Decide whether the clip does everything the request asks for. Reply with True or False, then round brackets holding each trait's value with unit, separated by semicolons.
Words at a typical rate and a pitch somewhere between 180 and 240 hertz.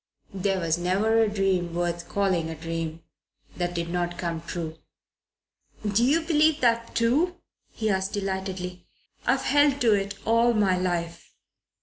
True (145 wpm; 190 Hz)